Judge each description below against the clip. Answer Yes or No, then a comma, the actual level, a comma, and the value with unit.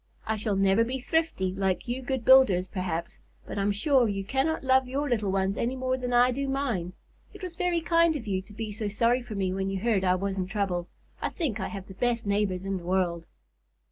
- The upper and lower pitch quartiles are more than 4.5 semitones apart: Yes, average, 5.2 semitones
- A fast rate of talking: Yes, fast, 235 wpm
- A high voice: Yes, high, 215 Hz